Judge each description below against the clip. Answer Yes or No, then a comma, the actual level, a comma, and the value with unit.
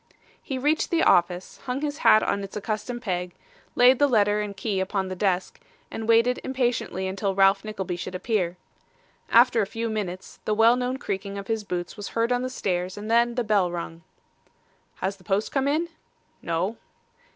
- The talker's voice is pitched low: No, high, 210 Hz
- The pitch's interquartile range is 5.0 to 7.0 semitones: No, average, 4.2 semitones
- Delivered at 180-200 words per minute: Yes, average, 185 wpm